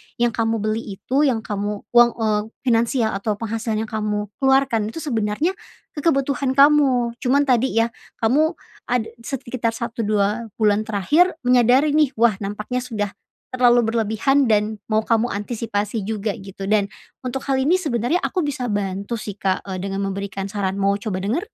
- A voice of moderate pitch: No, high, 225 Hz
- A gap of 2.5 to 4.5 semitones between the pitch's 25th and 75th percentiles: Yes, average, 3.6 semitones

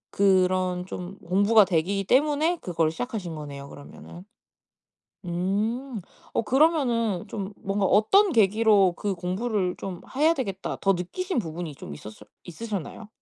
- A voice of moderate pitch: No, high, 195 Hz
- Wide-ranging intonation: No, average, 4.4 semitones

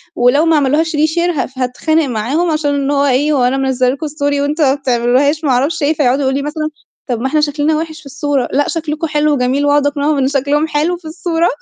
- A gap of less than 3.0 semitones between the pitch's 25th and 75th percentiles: Yes, narrow, 2.4 semitones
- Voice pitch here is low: No, very high, 290 Hz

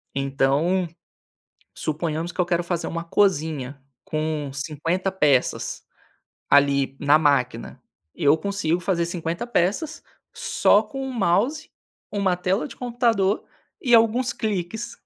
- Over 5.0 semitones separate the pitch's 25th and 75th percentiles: Yes, wide, 5.4 semitones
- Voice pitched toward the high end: No, medium, 175 Hz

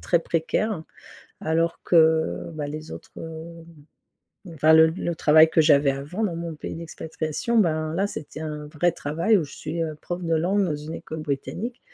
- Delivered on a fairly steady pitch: Yes, narrow, 1.8 semitones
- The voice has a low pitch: No, medium, 160 Hz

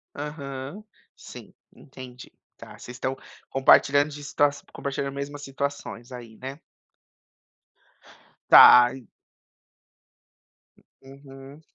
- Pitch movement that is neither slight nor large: No, narrow, 1.4 semitones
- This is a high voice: No, low, 135 Hz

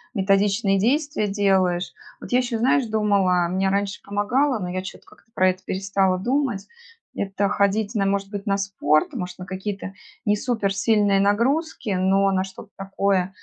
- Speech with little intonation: Yes, narrow, 1.8 semitones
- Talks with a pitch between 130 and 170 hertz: No, high, 200 Hz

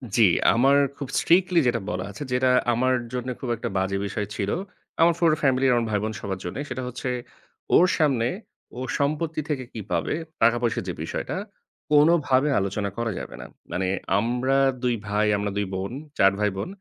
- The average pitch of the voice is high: No, low, 120 Hz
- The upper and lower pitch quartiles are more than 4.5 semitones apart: Yes, average, 4.9 semitones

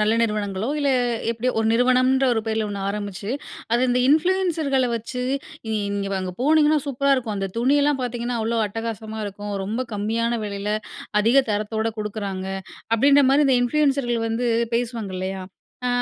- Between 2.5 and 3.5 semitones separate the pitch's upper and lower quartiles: No, average, 3.9 semitones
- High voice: Yes, high, 230 Hz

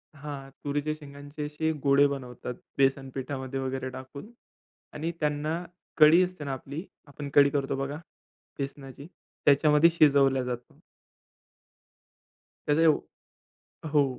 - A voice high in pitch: No, medium, 140 Hz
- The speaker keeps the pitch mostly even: Yes, narrow, 1.8 semitones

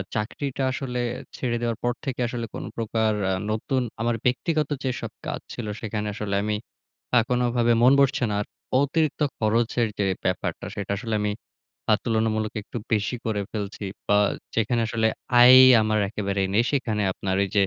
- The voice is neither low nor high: No, low, 115 Hz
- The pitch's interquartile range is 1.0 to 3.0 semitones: Yes, narrow, 2.6 semitones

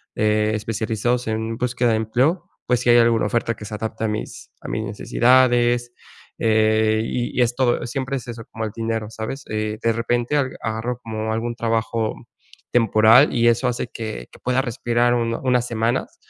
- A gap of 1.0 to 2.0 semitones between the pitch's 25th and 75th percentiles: Yes, narrow, 1.7 semitones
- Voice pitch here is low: Yes, low, 115 Hz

